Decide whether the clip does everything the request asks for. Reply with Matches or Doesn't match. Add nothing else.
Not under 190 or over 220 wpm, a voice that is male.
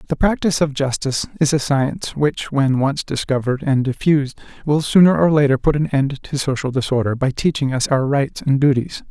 Matches